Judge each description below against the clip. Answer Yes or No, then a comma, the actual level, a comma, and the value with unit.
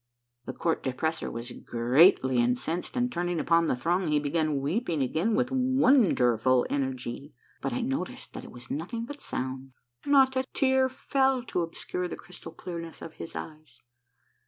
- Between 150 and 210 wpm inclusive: Yes, average, 165 wpm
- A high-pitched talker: No, medium, 165 Hz